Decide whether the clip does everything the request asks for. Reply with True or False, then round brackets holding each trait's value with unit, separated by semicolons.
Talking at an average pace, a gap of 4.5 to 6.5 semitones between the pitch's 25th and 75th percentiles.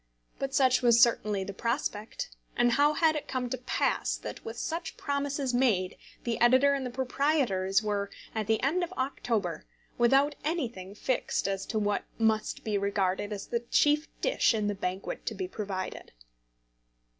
True (165 wpm; 5.1 semitones)